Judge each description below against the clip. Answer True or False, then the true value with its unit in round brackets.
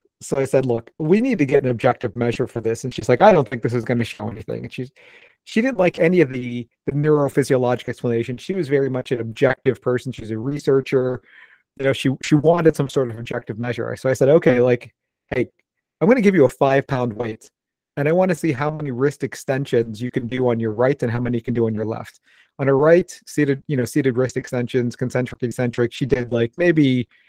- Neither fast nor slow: False (240 wpm)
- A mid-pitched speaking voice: False (130 Hz)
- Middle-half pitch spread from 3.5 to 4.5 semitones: False (3.0 semitones)